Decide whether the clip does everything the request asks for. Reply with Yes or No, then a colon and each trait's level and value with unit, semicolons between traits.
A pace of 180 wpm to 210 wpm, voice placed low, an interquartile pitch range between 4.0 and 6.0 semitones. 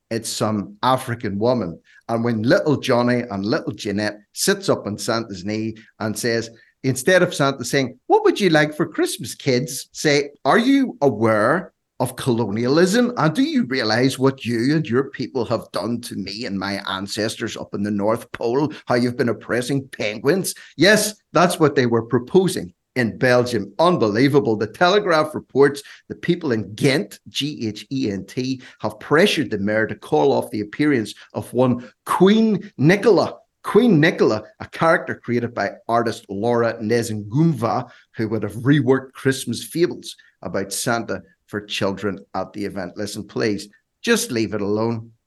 No: average, 165 wpm; low, 120 Hz; average, 4.7 semitones